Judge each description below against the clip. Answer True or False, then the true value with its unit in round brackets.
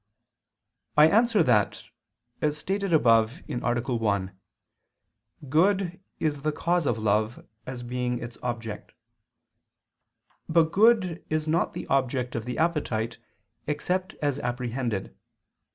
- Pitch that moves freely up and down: True (5.7 semitones)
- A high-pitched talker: False (130 Hz)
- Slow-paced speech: True (115 wpm)